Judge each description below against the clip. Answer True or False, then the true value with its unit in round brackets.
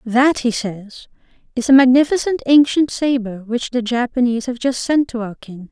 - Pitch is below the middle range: False (245 Hz)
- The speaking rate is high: False (180 wpm)